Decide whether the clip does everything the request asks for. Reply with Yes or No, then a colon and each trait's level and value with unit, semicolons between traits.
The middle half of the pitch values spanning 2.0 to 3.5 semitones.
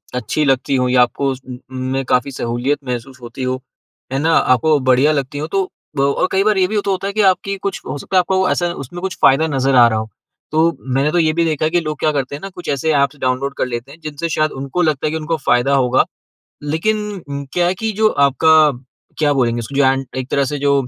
No: average, 4.3 semitones